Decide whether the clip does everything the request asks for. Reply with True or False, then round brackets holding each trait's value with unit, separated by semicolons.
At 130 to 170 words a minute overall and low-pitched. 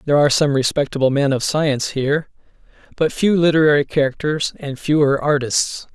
False (150 wpm; 145 Hz)